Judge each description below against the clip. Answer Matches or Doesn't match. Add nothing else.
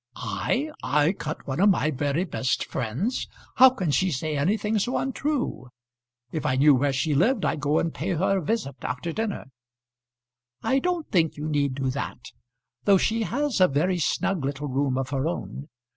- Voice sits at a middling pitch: Matches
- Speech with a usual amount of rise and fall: Doesn't match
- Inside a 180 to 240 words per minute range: Matches